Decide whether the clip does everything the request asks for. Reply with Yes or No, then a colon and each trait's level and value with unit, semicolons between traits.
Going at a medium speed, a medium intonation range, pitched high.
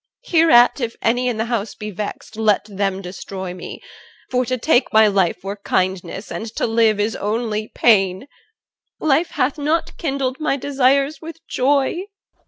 Yes: average, 160 wpm; average, 5.0 semitones; high, 230 Hz